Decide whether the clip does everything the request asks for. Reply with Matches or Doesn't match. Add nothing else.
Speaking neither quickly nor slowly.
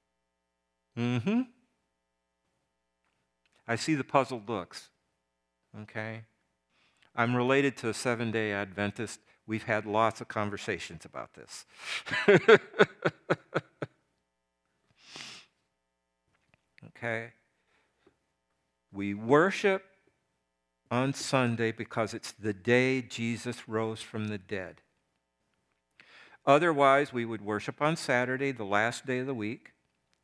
Doesn't match